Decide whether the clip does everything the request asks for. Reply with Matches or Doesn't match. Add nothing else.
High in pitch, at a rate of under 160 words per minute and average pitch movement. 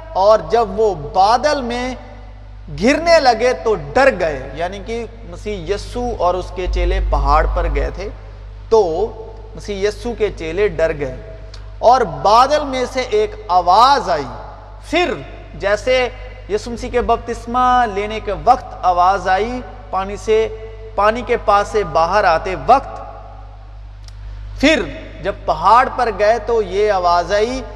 Doesn't match